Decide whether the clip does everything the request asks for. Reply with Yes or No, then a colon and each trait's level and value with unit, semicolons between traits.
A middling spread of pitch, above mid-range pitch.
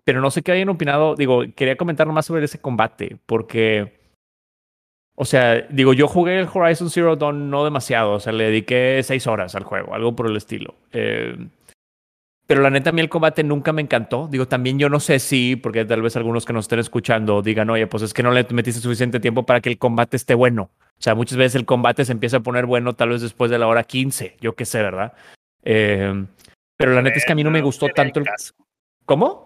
No: average, 3.9 semitones; low, 125 Hz